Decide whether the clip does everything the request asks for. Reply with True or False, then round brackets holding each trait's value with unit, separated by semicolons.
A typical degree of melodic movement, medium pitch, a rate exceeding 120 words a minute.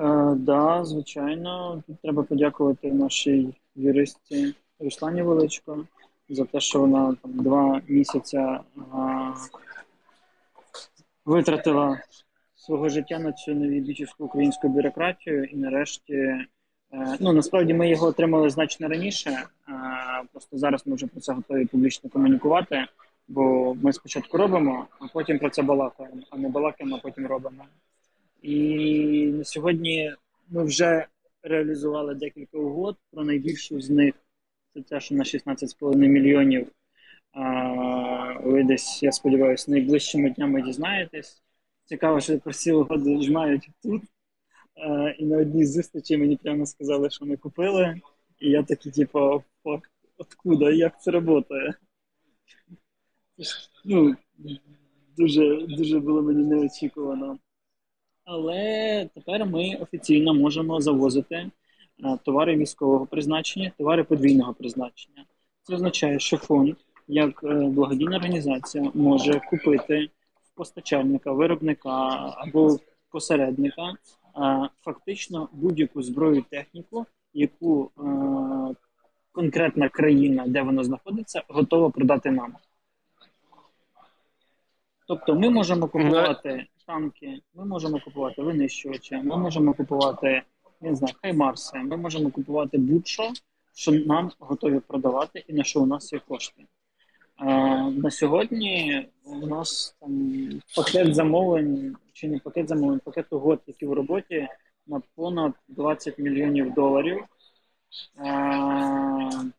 False (3.1 semitones; 150 Hz; 115 wpm)